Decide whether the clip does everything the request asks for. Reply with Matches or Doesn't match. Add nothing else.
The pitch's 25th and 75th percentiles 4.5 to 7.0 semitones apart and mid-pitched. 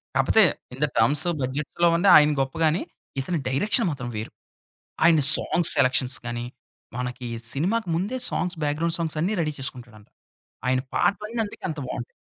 Matches